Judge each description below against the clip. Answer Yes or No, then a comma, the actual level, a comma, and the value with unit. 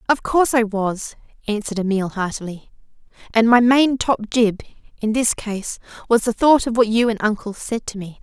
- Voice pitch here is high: Yes, high, 220 Hz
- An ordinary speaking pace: Yes, average, 190 wpm